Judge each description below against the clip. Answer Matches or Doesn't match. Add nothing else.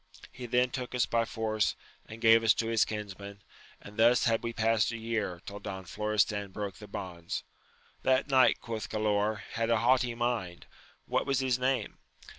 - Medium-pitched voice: Doesn't match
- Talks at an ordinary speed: Matches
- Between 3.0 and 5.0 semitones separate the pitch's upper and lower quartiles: Doesn't match